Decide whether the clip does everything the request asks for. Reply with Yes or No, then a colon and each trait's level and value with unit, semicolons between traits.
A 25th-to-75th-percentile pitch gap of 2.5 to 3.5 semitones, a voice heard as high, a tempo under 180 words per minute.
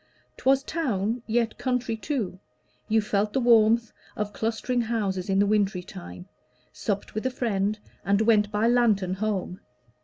Yes: average, 3.0 semitones; high, 215 Hz; average, 150 wpm